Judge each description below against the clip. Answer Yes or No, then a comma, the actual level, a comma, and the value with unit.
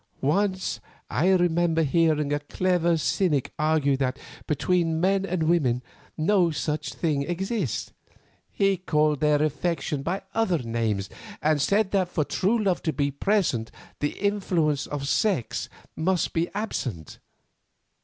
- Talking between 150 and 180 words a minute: No, slow, 135 wpm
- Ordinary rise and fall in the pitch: Yes, average, 4.3 semitones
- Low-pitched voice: No, medium, 160 Hz